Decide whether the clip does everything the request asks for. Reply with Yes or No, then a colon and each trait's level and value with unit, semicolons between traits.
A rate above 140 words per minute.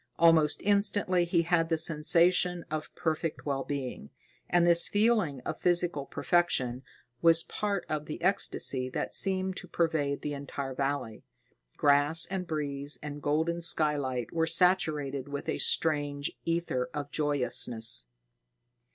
No: slow, 135 wpm